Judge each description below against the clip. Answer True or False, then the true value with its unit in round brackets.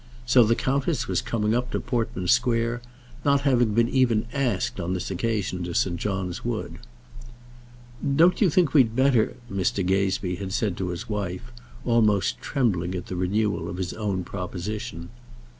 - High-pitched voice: False (105 Hz)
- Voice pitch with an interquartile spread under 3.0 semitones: False (4.8 semitones)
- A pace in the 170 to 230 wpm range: False (160 wpm)